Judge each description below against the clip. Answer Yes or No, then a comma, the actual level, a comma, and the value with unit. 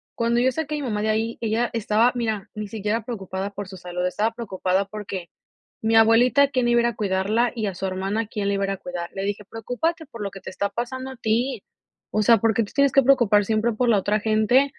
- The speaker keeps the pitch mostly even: No, average, 3.1 semitones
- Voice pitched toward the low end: No, high, 220 Hz